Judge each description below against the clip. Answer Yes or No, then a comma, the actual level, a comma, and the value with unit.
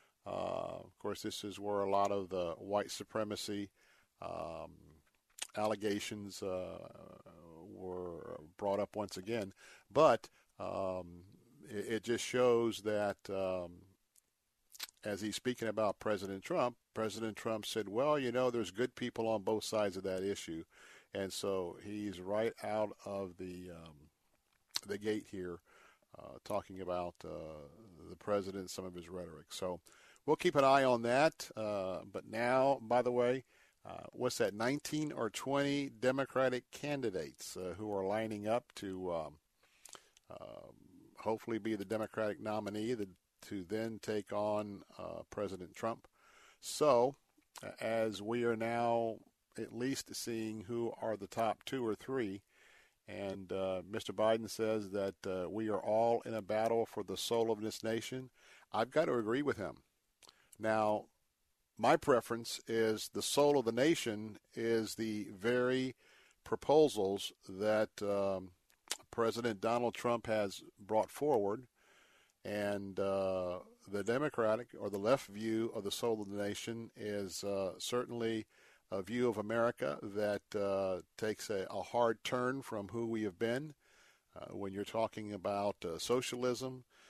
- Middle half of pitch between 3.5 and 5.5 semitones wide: No, average, 2.8 semitones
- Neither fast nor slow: Yes, average, 145 wpm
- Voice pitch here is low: Yes, low, 110 Hz